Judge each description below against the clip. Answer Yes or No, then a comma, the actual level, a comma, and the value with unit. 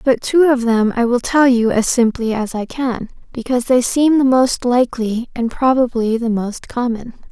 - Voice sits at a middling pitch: No, high, 245 Hz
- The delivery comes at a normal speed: Yes, average, 195 wpm